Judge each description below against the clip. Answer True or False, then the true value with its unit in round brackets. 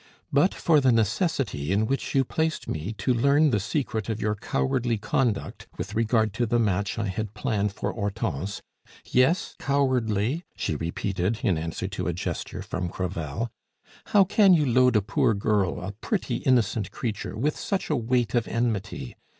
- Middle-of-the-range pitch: False (110 Hz)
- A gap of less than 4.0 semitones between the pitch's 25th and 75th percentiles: False (4.6 semitones)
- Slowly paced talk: False (170 wpm)